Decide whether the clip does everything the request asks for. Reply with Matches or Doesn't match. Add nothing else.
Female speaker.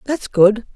Doesn't match